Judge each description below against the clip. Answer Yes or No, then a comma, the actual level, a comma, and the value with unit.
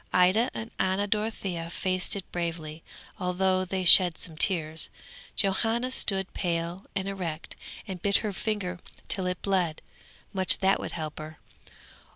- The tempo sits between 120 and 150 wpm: Yes, average, 145 wpm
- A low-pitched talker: No, medium, 185 Hz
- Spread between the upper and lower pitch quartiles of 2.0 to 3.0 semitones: Yes, narrow, 2.6 semitones